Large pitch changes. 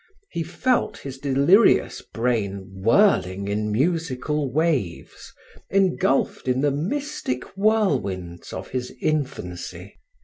Yes: wide, 8.2 semitones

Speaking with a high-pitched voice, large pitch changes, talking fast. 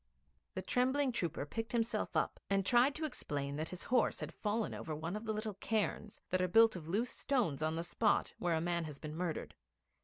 Yes: high, 195 Hz; wide, 5.8 semitones; fast, 215 wpm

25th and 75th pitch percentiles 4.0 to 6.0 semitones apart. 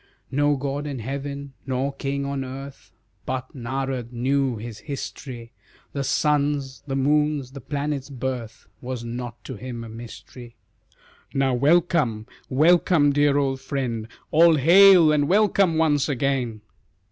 No: narrow, 2.5 semitones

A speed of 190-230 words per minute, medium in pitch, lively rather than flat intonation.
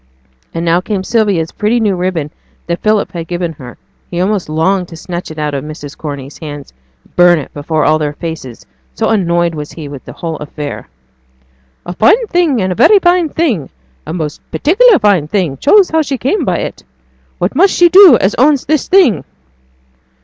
Yes: average, 195 wpm; medium, 175 Hz; wide, 7.7 semitones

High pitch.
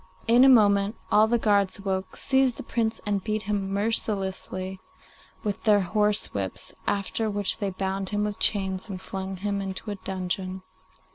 Yes: high, 200 Hz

